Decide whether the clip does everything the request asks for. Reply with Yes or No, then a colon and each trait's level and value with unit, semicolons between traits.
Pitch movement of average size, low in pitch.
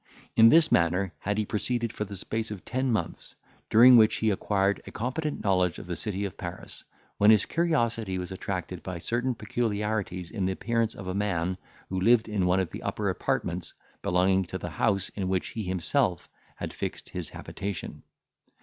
Yes: average, 3.6 semitones; low, 100 Hz